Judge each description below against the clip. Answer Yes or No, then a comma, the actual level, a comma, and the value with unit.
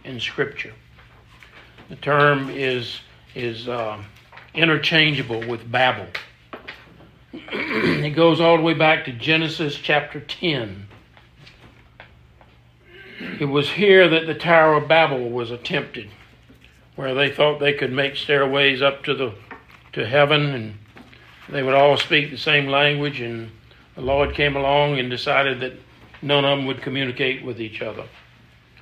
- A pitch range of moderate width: Yes, average, 3.4 semitones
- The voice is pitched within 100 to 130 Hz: No, medium, 140 Hz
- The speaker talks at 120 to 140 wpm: Yes, slow, 135 wpm